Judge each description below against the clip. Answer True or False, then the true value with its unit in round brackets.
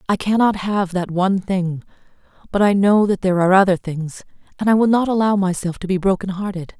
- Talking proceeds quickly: True (210 wpm)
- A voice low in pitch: False (190 Hz)